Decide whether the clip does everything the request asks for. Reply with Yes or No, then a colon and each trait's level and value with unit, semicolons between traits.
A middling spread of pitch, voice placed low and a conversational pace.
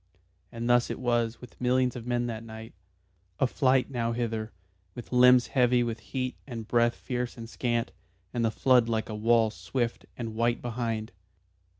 No: narrow, 1.5 semitones; low, 120 Hz; average, 170 wpm